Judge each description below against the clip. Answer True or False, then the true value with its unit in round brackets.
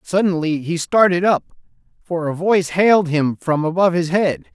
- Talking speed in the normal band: True (170 wpm)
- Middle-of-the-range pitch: True (175 Hz)